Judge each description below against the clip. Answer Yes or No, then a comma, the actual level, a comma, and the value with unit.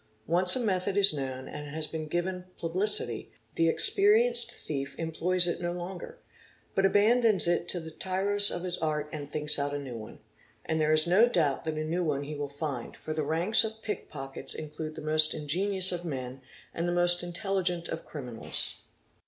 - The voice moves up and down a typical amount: Yes, average, 3.7 semitones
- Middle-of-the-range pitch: Yes, medium, 170 Hz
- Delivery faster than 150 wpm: Yes, average, 195 wpm